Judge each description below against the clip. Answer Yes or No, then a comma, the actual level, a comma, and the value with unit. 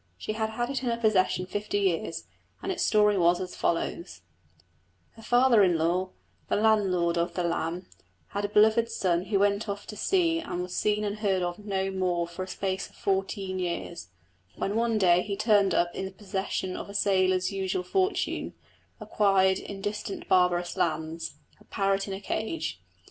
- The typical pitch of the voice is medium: No, high, 195 Hz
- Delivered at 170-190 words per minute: Yes, average, 185 wpm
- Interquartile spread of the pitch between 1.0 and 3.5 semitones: Yes, average, 2.8 semitones